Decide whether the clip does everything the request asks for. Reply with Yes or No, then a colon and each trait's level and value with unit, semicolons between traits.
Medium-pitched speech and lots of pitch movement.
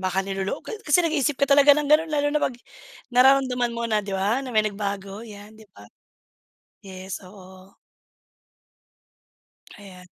No: high, 215 Hz; wide, 5.8 semitones